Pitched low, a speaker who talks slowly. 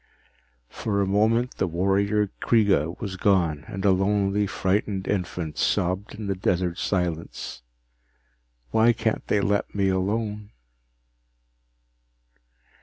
Yes: low, 100 Hz; slow, 110 wpm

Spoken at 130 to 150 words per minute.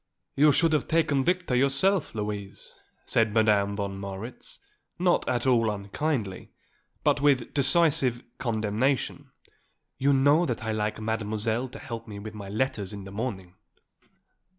Yes: average, 140 wpm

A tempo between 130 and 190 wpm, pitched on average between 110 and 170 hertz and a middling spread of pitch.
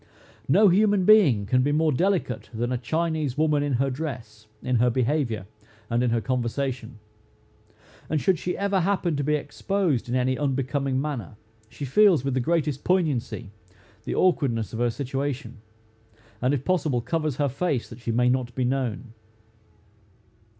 Yes: average, 165 wpm; low, 135 Hz; average, 4.4 semitones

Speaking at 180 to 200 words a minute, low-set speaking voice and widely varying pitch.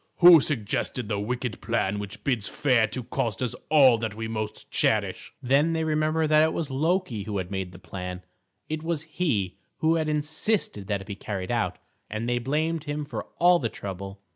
Yes: average, 195 wpm; low, 125 Hz; wide, 7.0 semitones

